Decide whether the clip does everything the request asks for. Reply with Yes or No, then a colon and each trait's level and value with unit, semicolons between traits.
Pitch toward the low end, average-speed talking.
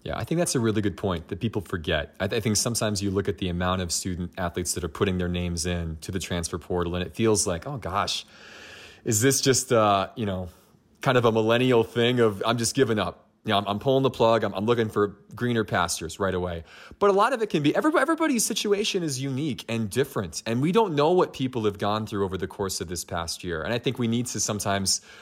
No: low, 110 Hz; fast, 255 wpm